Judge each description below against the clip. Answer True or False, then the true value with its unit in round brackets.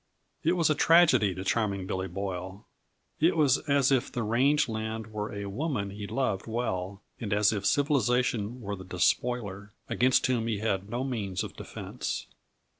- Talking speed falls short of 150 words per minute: False (170 wpm)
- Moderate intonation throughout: True (4.4 semitones)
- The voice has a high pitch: False (110 Hz)